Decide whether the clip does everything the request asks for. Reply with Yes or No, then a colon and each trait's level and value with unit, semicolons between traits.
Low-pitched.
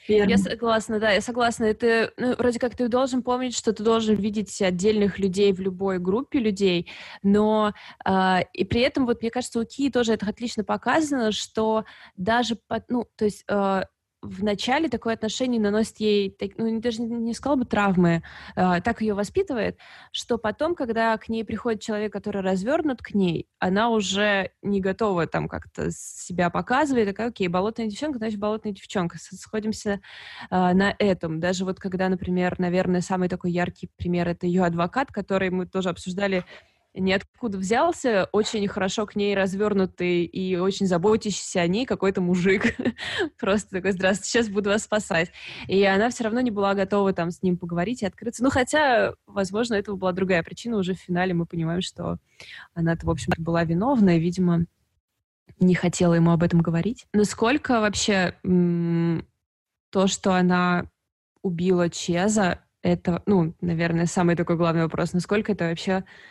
No: high, 200 Hz